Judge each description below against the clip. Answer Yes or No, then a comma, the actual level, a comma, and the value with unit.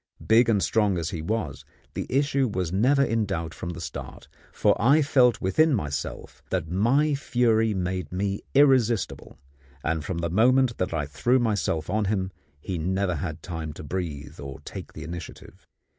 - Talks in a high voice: No, very low, 95 Hz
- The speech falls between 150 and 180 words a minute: Yes, average, 175 wpm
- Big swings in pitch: Yes, wide, 6.4 semitones